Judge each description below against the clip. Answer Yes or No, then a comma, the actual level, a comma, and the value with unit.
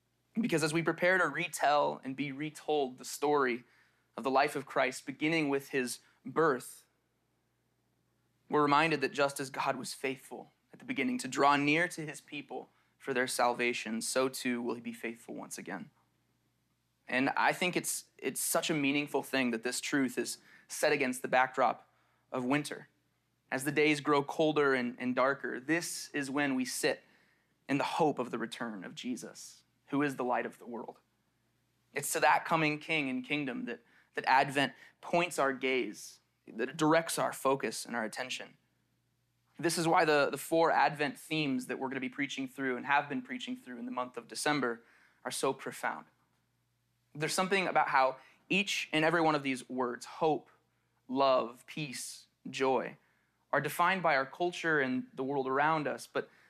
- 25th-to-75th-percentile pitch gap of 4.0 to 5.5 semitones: No, average, 3.3 semitones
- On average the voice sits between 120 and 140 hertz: Yes, low, 135 Hz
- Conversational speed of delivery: Yes, average, 180 wpm